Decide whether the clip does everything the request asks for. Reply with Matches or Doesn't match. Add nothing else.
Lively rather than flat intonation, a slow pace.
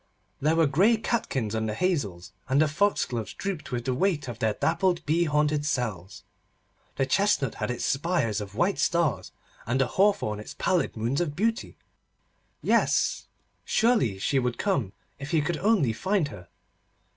Doesn't match